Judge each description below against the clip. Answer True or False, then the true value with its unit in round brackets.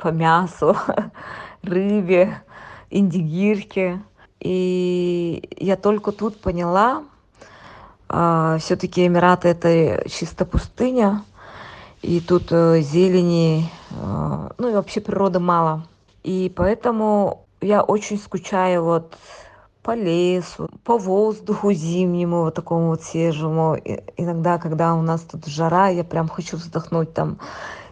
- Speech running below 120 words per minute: True (110 wpm)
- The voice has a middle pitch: True (180 Hz)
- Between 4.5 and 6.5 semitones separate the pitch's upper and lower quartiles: False (2.9 semitones)